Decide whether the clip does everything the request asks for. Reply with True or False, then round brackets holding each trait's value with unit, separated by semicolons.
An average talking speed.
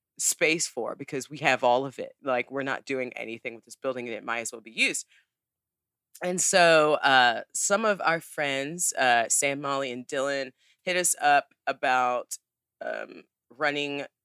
True (175 wpm)